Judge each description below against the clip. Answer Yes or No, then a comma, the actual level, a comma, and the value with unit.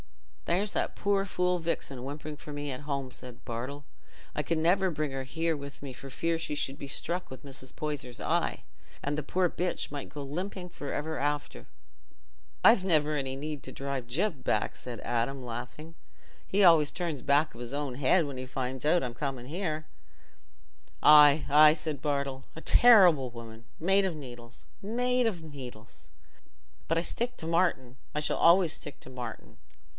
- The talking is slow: No, average, 175 wpm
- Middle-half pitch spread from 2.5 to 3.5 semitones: No, average, 4.1 semitones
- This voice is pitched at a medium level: Yes, medium, 145 Hz